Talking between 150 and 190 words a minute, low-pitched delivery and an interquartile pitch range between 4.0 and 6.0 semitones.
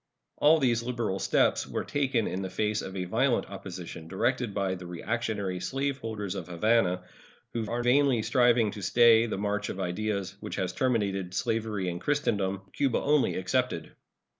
Yes: average, 165 wpm; low, 110 Hz; average, 4.4 semitones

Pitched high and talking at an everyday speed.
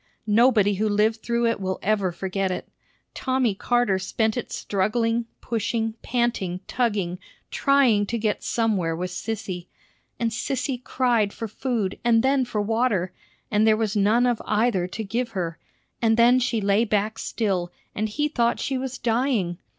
Yes: high, 220 Hz; average, 160 wpm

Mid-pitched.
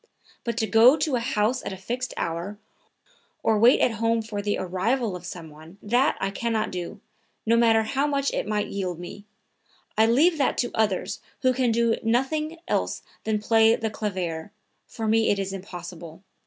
No: high, 220 Hz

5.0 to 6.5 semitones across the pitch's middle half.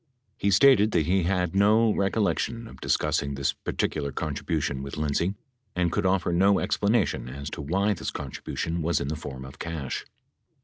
Yes: average, 5.3 semitones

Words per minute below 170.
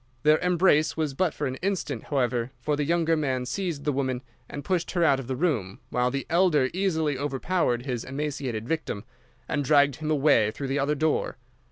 No: average, 195 wpm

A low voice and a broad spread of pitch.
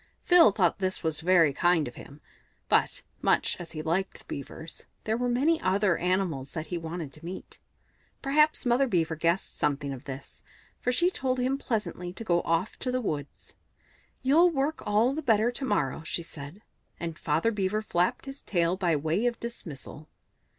No: medium, 185 Hz; wide, 7.1 semitones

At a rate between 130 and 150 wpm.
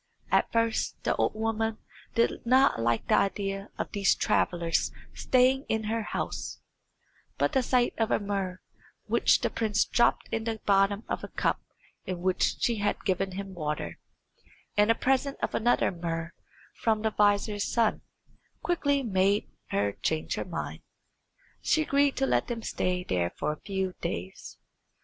No: average, 160 wpm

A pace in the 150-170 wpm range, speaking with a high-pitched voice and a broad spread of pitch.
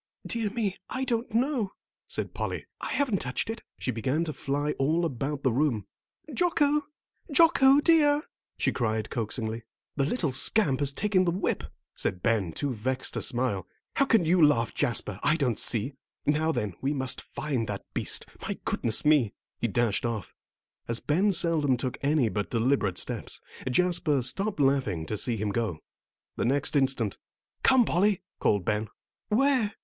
No: average, 165 wpm; medium, 140 Hz; wide, 9.0 semitones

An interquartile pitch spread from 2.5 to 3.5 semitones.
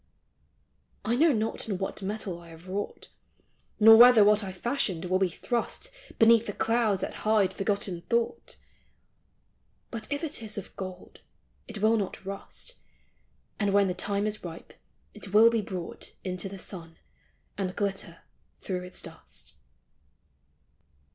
Yes: average, 3.1 semitones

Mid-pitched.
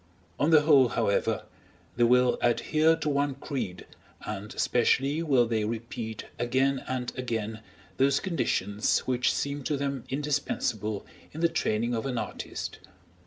No: low, 125 Hz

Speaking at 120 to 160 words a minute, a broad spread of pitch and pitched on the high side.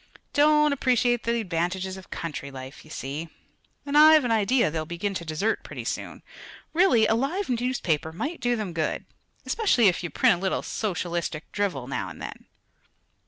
No: average, 170 wpm; wide, 7.1 semitones; high, 205 Hz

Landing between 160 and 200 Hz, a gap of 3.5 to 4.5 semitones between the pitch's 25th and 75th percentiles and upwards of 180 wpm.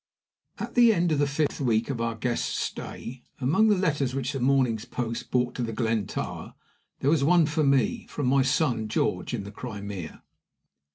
No: low, 130 Hz; average, 4.2 semitones; average, 190 wpm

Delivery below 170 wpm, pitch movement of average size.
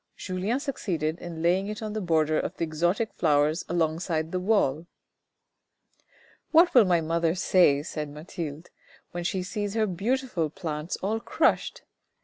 Yes: average, 160 wpm; average, 4.4 semitones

